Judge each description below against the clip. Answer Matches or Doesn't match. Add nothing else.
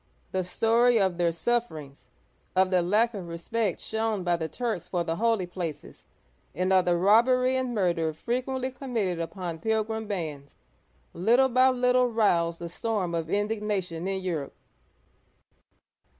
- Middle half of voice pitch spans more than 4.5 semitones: Matches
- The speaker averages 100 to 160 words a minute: Matches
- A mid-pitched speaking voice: Doesn't match